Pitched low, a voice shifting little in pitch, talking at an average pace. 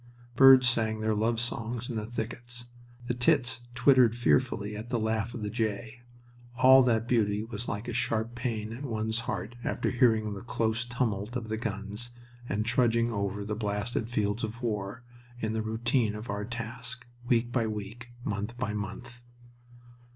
Yes: low, 115 Hz; narrow, 2.1 semitones; average, 170 wpm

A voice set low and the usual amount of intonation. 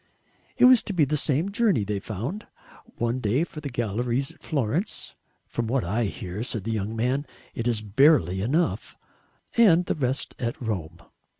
No: low, 120 Hz; wide, 6.0 semitones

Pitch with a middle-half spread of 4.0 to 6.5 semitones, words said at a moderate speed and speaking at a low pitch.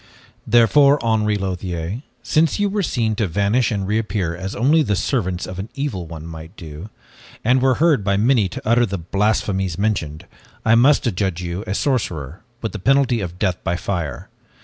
Yes: average, 5.1 semitones; average, 185 wpm; low, 105 Hz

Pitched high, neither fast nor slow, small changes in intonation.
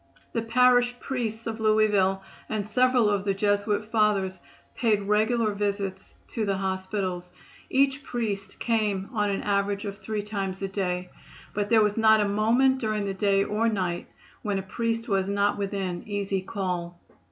Yes: high, 205 Hz; average, 165 wpm; narrow, 2.3 semitones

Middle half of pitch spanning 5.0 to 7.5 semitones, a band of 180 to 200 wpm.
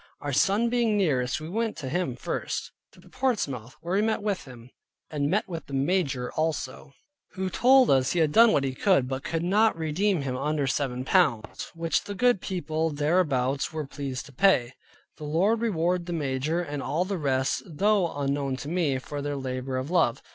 Yes: wide, 5.5 semitones; average, 190 wpm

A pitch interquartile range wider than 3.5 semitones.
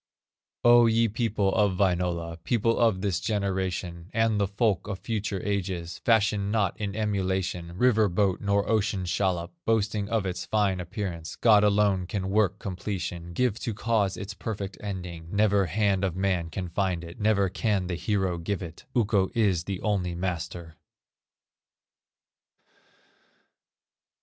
No: average, 2.7 semitones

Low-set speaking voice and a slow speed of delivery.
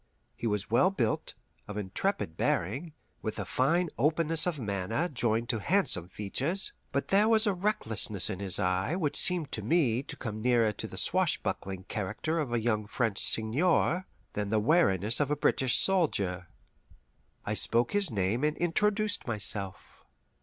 No: low, 120 Hz; average, 160 wpm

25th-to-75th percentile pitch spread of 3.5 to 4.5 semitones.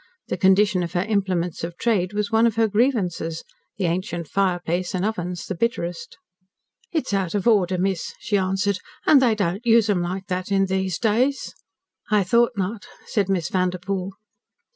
No: average, 2.9 semitones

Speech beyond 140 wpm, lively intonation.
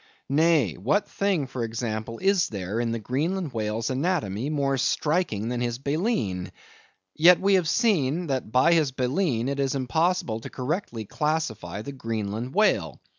Yes: average, 155 wpm; wide, 6.5 semitones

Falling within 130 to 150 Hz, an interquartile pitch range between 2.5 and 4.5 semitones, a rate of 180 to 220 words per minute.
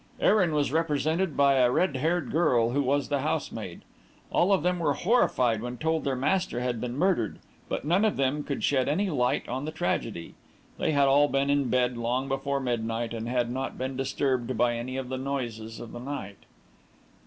Yes: low, 135 Hz; average, 3.5 semitones; average, 200 wpm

